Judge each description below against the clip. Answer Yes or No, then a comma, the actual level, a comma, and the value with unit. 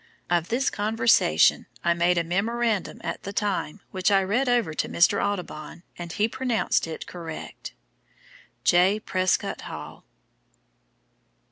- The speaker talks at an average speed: No, slow, 130 wpm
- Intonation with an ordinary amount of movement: Yes, average, 4.3 semitones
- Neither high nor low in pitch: No, high, 195 Hz